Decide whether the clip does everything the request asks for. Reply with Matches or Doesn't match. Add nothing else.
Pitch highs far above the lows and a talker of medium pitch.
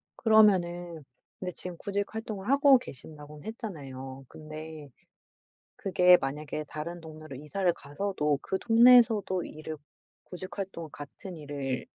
Doesn't match